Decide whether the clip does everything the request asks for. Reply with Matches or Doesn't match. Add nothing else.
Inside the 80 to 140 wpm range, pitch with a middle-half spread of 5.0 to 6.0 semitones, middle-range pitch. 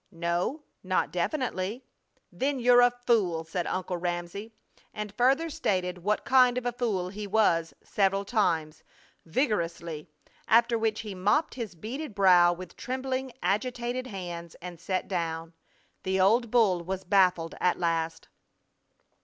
Doesn't match